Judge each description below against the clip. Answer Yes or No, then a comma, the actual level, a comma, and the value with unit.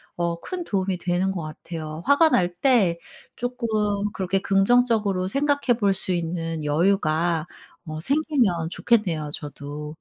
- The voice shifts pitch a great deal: Yes, wide, 6.1 semitones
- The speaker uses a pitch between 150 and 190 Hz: Yes, medium, 185 Hz